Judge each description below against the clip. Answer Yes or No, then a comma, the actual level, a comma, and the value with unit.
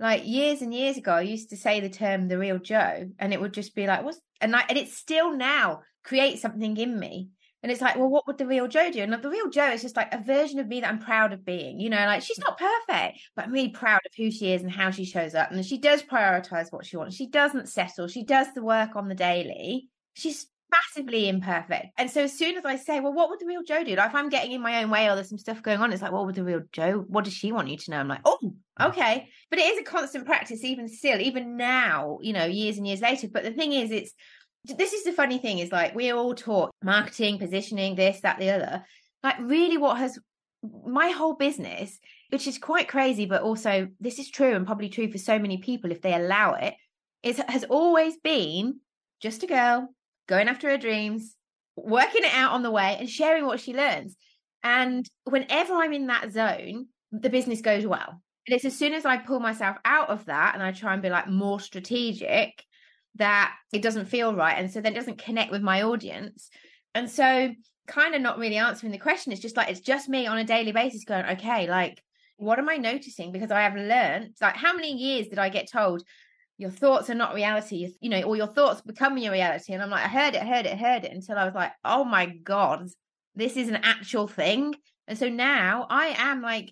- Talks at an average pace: No, fast, 245 wpm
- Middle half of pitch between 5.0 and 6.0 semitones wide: Yes, average, 5.3 semitones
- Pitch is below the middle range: No, high, 230 Hz